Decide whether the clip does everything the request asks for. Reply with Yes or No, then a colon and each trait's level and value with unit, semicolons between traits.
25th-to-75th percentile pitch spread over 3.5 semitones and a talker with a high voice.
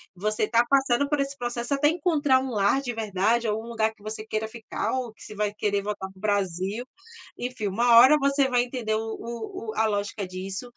No: average, 3.2 semitones; high, 225 Hz